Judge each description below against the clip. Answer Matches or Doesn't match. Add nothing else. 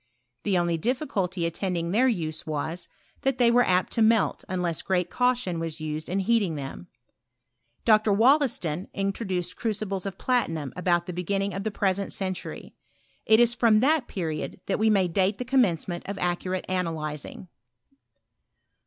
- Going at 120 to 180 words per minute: Matches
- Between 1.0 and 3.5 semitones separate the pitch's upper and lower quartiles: Doesn't match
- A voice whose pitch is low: Doesn't match